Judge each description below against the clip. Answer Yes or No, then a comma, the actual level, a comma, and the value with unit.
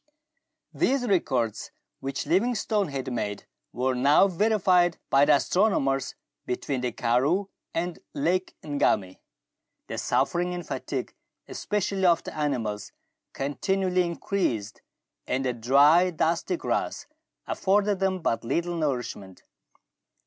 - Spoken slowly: Yes, slow, 110 wpm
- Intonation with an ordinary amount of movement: No, wide, 6.3 semitones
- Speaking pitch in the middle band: Yes, medium, 165 Hz